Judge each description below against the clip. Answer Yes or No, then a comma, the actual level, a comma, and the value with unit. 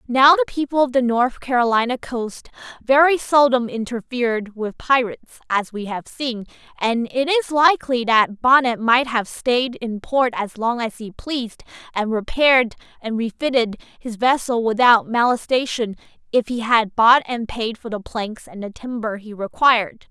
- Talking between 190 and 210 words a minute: No, average, 160 wpm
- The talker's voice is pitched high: Yes, high, 240 Hz